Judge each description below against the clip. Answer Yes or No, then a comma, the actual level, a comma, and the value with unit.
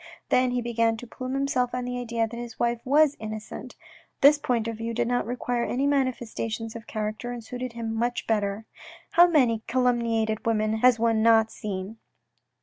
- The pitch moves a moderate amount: No, narrow, 1.9 semitones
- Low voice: No, high, 235 Hz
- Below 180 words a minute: No, average, 185 wpm